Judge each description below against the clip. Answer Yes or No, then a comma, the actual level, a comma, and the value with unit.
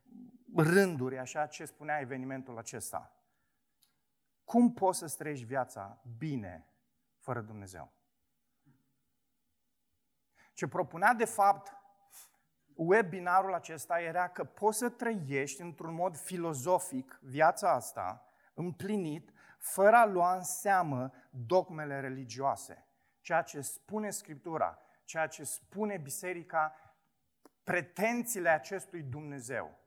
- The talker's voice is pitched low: No, medium, 165 Hz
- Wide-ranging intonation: Yes, wide, 5.8 semitones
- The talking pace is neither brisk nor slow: No, slow, 100 wpm